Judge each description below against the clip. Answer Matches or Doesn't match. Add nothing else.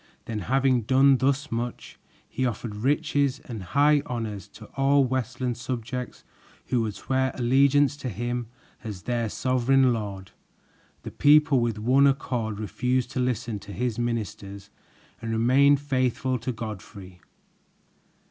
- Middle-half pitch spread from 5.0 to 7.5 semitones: Doesn't match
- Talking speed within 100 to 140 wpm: Matches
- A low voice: Matches